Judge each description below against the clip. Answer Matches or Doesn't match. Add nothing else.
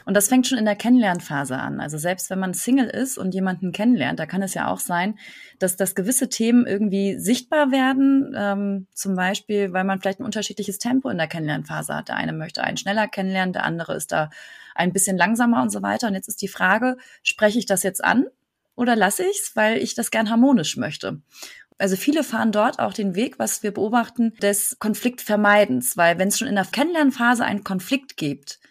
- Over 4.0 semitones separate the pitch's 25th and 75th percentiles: Matches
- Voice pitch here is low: Doesn't match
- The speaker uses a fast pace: Matches